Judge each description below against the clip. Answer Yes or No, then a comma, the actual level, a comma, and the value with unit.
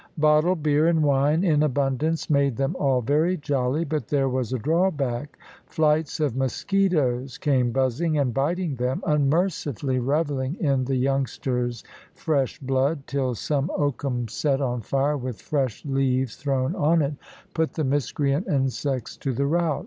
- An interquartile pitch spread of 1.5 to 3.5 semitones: Yes, average, 2.7 semitones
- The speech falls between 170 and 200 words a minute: No, average, 150 wpm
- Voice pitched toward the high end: No, medium, 140 Hz